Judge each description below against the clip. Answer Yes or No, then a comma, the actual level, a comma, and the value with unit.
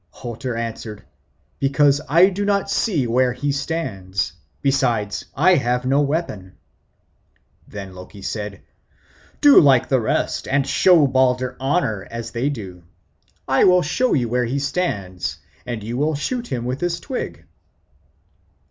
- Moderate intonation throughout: Yes, average, 5.0 semitones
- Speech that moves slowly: No, average, 150 wpm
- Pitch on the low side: Yes, low, 130 Hz